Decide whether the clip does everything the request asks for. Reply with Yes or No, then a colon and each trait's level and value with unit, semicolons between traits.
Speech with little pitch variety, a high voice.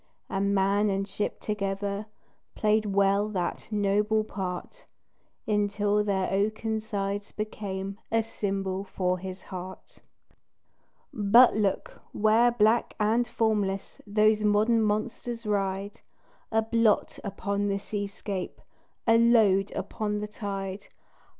Yes: narrow, 1.7 semitones; high, 205 Hz